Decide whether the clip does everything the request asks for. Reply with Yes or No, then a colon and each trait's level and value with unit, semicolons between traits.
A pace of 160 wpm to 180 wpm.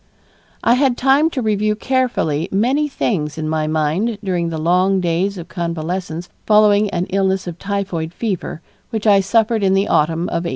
Yes: average, 175 wpm